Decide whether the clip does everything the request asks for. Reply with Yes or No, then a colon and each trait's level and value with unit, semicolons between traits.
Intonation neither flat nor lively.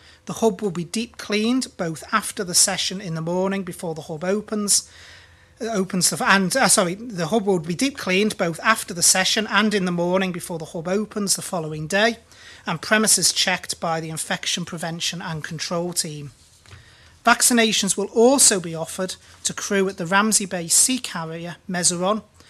Yes: average, 3.7 semitones